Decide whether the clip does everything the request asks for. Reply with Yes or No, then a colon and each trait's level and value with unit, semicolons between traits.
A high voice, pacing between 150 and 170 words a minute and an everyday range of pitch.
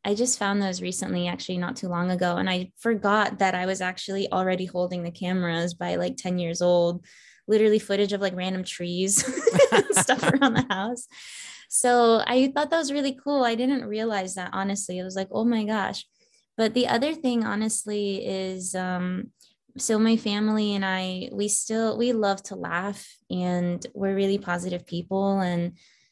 No: high, 195 Hz; average, 180 wpm; average, 3.9 semitones